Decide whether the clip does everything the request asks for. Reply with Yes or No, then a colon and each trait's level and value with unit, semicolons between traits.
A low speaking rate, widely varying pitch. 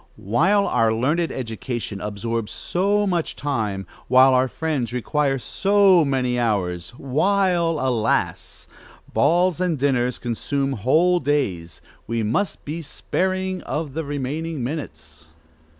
Yes: slow, 120 wpm; wide, 6.2 semitones